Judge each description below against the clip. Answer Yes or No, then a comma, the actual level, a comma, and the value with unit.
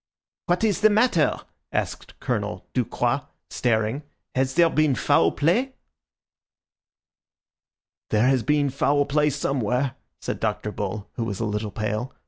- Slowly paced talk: Yes, slow, 130 wpm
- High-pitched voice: No, low, 135 Hz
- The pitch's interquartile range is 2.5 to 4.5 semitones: No, wide, 5.6 semitones